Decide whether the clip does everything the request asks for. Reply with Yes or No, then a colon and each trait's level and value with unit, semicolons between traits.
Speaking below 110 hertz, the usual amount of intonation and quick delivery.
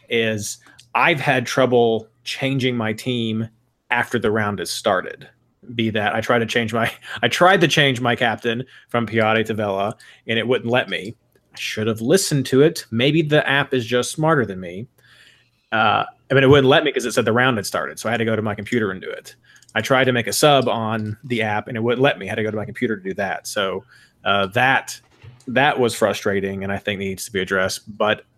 No: low, 115 Hz; average, 3.0 semitones; fast, 235 wpm